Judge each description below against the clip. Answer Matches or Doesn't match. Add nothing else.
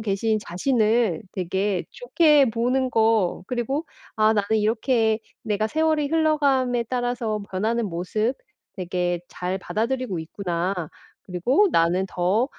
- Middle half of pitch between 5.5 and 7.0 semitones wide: Doesn't match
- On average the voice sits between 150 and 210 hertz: Doesn't match